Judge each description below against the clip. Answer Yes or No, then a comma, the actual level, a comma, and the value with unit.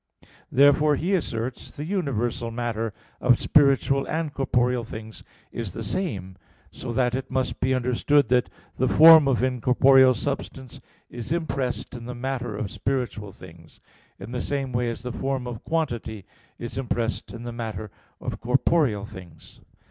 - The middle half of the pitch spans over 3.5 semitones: No, average, 3.0 semitones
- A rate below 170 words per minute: Yes, average, 155 wpm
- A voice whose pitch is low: Yes, low, 125 Hz